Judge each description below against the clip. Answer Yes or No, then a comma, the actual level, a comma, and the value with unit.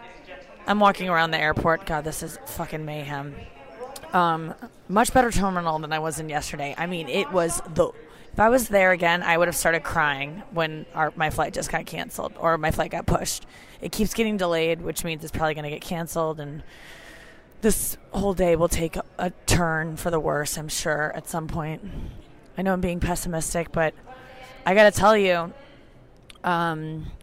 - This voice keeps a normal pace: Yes, average, 190 wpm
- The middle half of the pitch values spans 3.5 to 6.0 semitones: No, narrow, 2.6 semitones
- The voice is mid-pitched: Yes, medium, 165 Hz